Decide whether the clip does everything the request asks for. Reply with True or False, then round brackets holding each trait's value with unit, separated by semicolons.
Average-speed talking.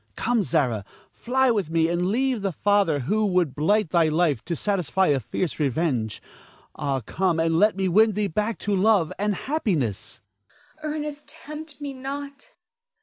True (165 wpm)